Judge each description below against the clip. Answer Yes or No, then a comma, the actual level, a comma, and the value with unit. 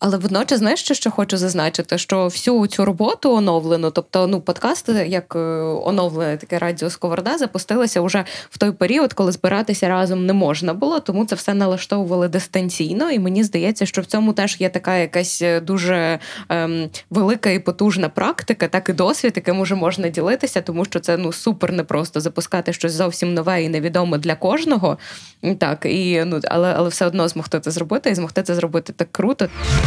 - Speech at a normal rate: No, fast, 185 wpm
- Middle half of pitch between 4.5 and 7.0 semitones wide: No, average, 2.9 semitones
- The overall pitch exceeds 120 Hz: Yes, medium, 185 Hz